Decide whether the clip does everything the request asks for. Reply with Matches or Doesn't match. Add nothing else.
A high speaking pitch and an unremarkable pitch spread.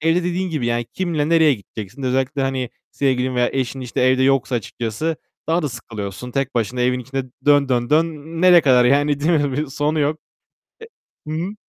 Doesn't match